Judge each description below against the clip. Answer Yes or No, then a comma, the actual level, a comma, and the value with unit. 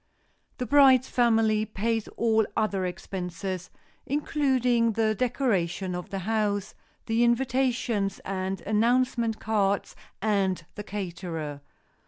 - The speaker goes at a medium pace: No, slow, 105 wpm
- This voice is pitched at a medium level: No, high, 215 Hz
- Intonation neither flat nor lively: Yes, average, 3.7 semitones